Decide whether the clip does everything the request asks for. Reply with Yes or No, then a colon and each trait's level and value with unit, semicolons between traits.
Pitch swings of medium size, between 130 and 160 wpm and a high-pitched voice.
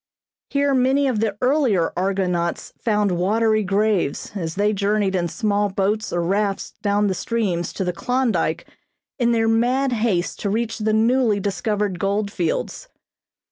Yes: average, 3.0 semitones; average, 150 wpm; high, 210 Hz